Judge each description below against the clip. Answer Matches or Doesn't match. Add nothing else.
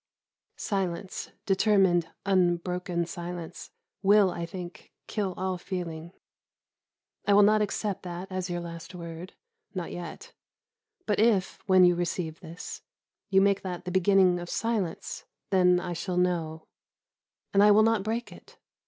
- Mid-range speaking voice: Matches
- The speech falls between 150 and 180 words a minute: Doesn't match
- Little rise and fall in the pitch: Matches